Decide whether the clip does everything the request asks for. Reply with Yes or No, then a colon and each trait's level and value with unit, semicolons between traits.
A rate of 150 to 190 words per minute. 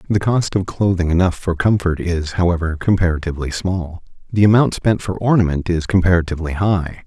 Yes: average, 160 wpm